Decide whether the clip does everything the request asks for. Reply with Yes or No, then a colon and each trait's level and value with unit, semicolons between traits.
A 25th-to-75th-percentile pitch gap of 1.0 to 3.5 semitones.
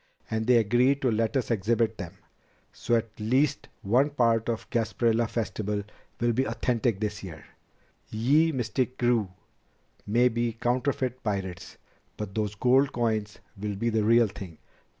Yes: narrow, 2.6 semitones